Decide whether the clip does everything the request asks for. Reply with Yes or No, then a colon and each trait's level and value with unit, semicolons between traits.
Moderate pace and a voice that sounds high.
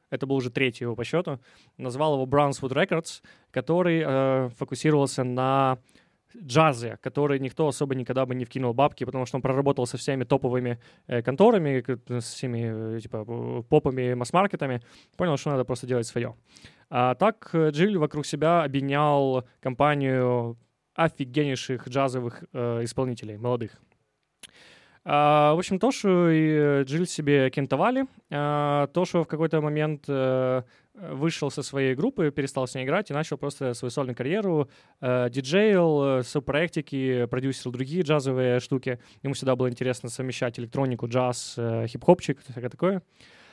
No: average, 140 wpm; low, 135 Hz